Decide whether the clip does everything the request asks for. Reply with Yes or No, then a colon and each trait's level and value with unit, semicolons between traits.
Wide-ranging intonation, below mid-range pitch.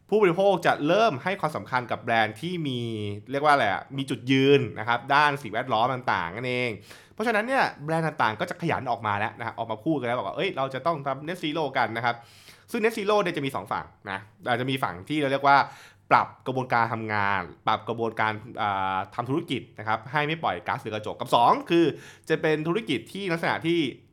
Yes: wide, 6.1 semitones; low, 130 Hz